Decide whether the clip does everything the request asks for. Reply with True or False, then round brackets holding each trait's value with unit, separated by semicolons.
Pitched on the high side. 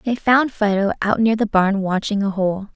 True (210 Hz)